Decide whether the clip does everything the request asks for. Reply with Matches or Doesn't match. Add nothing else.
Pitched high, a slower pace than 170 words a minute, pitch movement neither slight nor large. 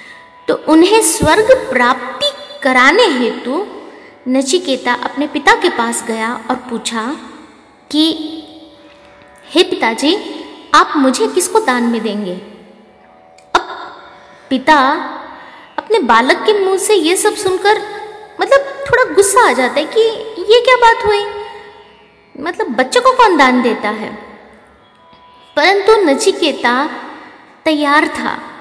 Doesn't match